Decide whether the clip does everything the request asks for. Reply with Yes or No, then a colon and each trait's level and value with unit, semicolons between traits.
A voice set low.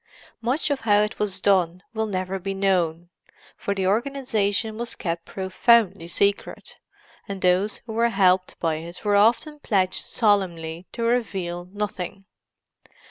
No: high, 195 Hz